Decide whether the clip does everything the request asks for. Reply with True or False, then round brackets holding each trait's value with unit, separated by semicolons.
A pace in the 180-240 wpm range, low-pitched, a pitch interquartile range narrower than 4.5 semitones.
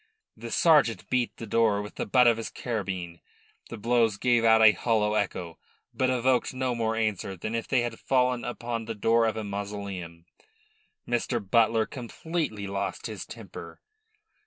False (165 wpm; 115 Hz; 3.0 semitones)